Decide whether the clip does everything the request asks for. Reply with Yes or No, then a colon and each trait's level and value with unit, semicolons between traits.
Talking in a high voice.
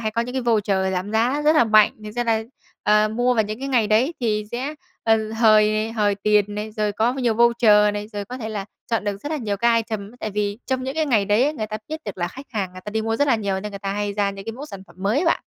Yes: high, 215 Hz